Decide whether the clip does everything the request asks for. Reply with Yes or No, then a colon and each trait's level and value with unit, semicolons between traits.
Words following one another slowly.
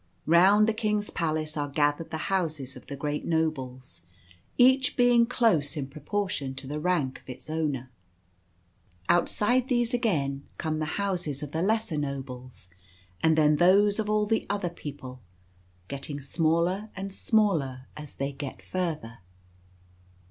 No: average, 145 wpm